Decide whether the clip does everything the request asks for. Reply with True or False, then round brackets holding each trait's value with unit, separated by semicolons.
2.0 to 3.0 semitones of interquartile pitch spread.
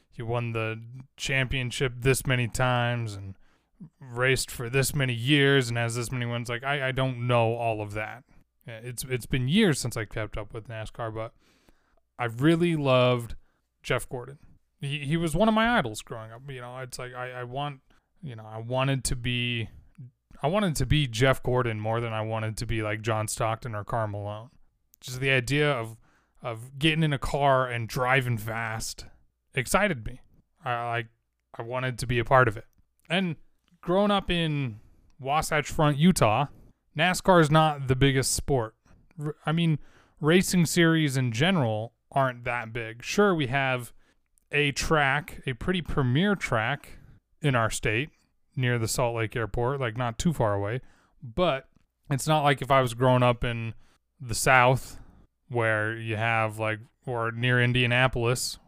False (3.8 semitones)